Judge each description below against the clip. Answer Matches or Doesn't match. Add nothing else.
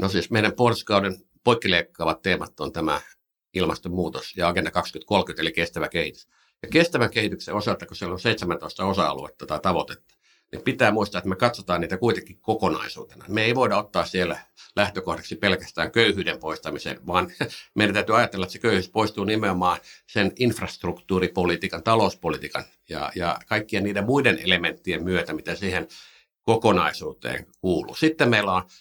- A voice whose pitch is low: Matches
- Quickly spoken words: Doesn't match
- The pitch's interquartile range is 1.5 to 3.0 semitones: Doesn't match